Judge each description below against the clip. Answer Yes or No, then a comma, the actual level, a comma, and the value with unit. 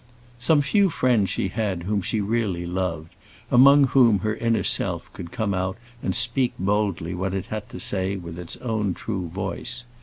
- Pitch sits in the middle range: No, low, 100 Hz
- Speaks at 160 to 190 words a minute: Yes, average, 180 wpm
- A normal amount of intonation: Yes, average, 4.2 semitones